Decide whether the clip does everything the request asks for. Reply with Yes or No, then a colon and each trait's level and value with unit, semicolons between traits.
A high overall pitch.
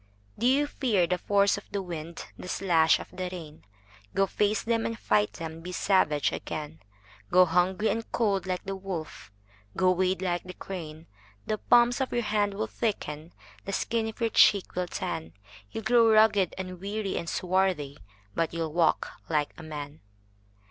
No: medium, 180 Hz